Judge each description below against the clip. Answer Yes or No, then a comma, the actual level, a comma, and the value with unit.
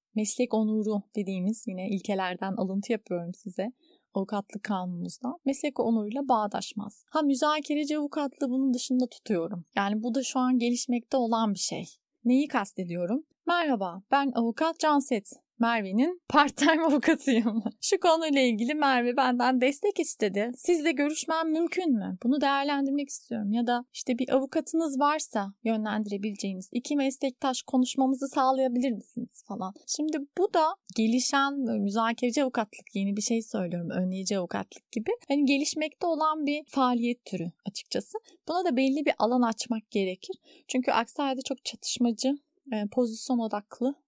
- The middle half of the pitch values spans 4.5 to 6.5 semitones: Yes, average, 5.0 semitones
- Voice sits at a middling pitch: No, very high, 250 Hz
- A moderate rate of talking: Yes, average, 130 wpm